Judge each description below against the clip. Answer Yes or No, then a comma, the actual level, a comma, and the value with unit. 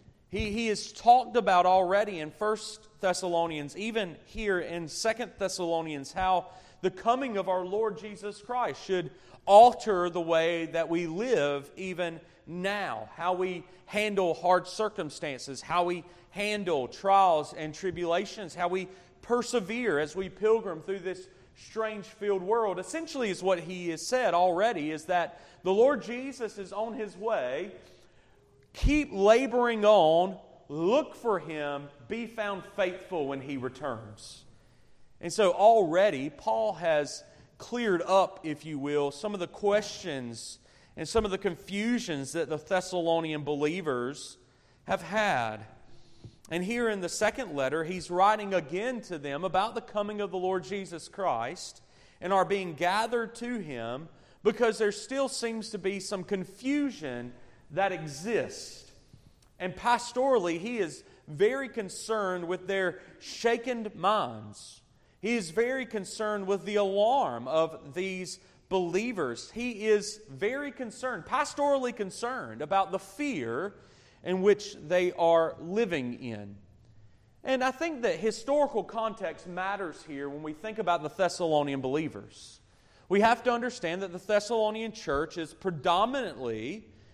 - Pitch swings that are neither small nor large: Yes, average, 4.8 semitones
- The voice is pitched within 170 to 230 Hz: Yes, medium, 185 Hz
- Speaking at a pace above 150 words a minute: No, average, 140 wpm